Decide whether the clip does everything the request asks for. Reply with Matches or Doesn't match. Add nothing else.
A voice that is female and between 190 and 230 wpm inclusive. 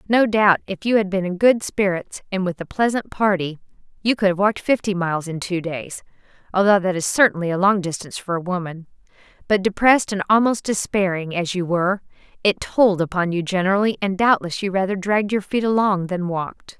Matches